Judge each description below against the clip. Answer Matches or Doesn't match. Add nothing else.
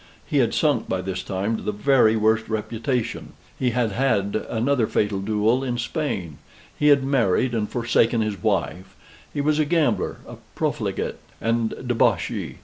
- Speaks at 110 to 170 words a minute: Matches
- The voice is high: Doesn't match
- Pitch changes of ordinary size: Matches